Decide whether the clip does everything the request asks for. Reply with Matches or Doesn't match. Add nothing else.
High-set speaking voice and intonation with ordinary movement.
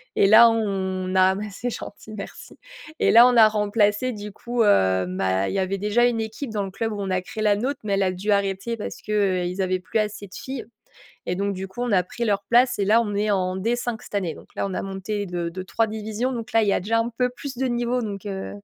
Matches